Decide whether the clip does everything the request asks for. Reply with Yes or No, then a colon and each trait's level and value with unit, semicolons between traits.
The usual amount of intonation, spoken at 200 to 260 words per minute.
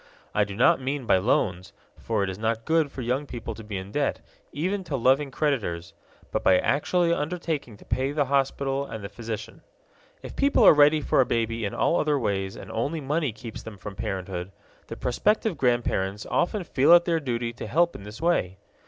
No: wide, 6.0 semitones; fast, 205 wpm